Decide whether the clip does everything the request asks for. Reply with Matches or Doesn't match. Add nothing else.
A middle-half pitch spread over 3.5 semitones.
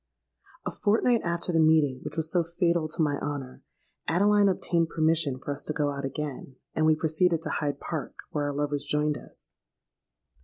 Doesn't match